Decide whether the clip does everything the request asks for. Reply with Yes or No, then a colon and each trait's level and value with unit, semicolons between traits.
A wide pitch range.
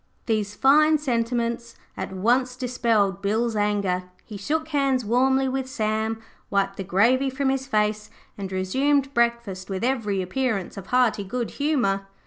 No: average, 4.7 semitones